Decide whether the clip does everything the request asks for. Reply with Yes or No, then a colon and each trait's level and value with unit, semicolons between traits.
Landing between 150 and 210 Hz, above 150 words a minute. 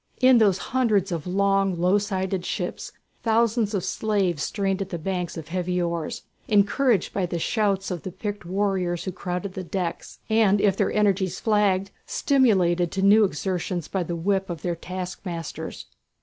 Yes: high, 190 Hz; average, 165 wpm